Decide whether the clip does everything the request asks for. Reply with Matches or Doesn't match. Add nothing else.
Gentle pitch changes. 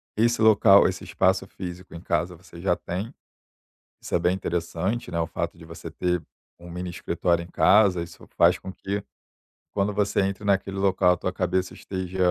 Matches